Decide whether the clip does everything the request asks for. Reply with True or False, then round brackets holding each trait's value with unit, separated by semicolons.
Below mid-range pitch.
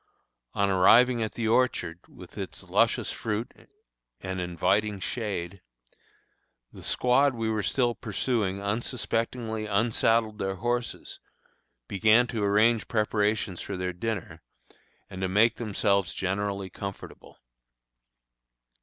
True (105 Hz)